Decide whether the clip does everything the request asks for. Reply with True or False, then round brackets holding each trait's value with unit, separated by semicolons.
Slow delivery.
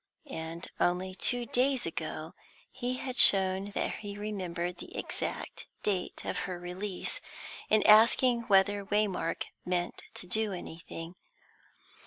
True (125 wpm)